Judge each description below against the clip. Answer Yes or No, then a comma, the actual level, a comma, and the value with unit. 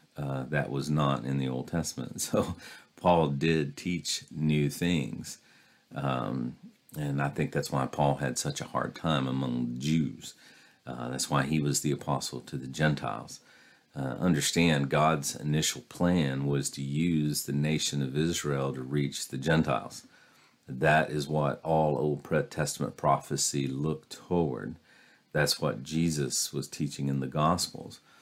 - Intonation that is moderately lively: No, narrow, 2.2 semitones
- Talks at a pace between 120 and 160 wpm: Yes, average, 150 wpm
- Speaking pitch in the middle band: No, very low, 75 Hz